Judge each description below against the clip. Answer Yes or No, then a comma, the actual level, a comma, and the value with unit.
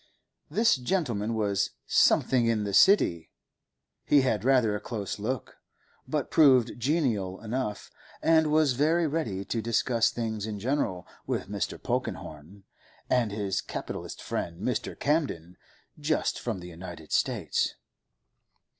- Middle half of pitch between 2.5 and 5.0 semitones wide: No, wide, 5.5 semitones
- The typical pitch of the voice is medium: No, low, 115 Hz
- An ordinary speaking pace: No, slow, 130 wpm